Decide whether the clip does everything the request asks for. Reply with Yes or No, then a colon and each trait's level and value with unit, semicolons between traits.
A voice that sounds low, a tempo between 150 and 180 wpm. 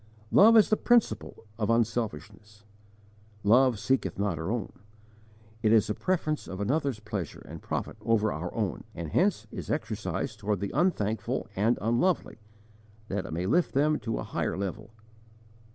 Yes: low, 110 Hz; average, 155 wpm